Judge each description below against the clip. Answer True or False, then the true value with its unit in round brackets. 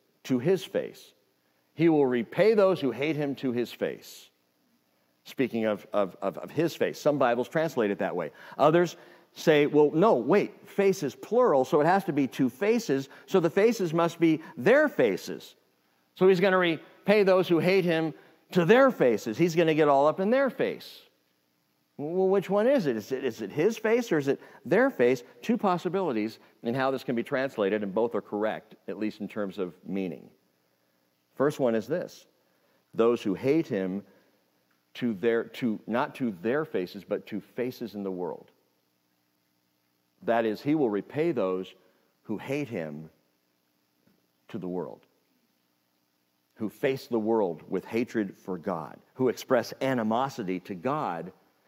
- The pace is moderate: True (170 wpm)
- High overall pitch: False (120 Hz)